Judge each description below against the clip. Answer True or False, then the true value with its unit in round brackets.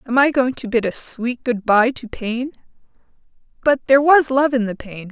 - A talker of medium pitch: False (245 Hz)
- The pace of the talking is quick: True (210 wpm)